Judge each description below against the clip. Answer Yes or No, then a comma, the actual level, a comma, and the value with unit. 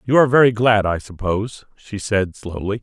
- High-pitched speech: No, low, 105 Hz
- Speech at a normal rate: Yes, average, 190 wpm